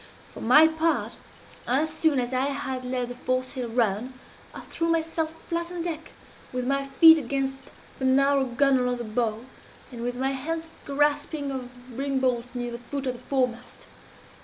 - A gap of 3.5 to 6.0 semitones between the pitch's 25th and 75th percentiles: No, average, 2.9 semitones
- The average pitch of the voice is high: Yes, very high, 265 Hz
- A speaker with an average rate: Yes, average, 175 wpm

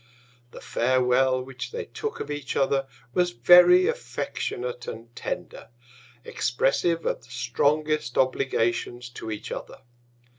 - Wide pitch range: No, average, 4.1 semitones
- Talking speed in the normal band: No, slow, 120 wpm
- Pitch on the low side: Yes, low, 130 Hz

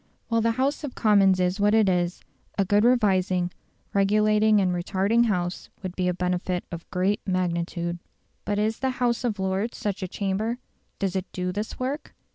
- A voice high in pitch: Yes, high, 195 Hz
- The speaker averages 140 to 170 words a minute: No, average, 180 wpm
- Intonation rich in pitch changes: No, average, 3.1 semitones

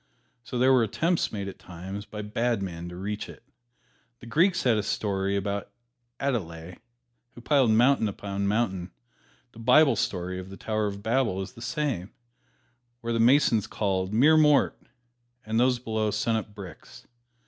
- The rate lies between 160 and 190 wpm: Yes, average, 170 wpm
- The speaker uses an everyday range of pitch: Yes, average, 3.9 semitones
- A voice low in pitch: Yes, low, 110 Hz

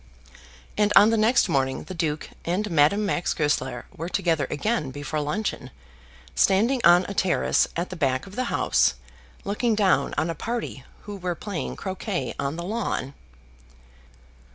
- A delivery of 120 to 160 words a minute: Yes, average, 155 wpm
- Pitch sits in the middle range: Yes, medium, 175 Hz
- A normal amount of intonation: No, wide, 5.9 semitones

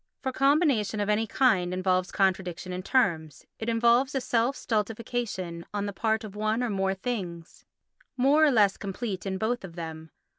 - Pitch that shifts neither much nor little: Yes, average, 4.6 semitones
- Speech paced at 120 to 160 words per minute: No, average, 175 wpm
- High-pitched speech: Yes, high, 210 Hz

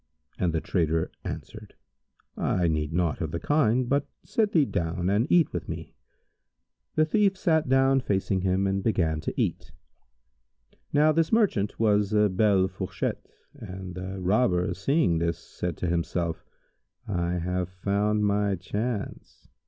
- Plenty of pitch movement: Yes, wide, 5.8 semitones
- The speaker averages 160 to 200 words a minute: No, average, 145 wpm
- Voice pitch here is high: No, very low, 95 Hz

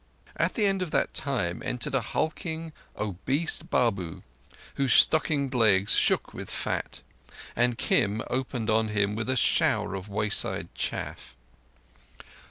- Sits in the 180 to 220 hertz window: No, low, 120 Hz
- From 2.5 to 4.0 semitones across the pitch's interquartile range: No, average, 5.1 semitones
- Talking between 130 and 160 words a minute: Yes, slow, 135 wpm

